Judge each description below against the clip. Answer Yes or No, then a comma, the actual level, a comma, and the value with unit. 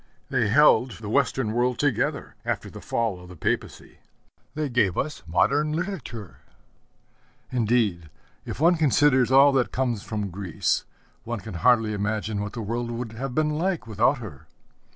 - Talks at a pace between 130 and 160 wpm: Yes, average, 155 wpm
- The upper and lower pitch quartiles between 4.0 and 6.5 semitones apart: Yes, average, 4.5 semitones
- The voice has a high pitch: No, low, 120 Hz